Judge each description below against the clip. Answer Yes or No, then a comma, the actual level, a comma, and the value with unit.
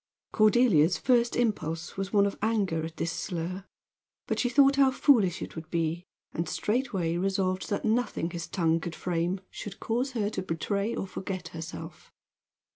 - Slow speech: No, average, 165 wpm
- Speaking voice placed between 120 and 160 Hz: No, high, 190 Hz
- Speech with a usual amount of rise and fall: Yes, average, 5.0 semitones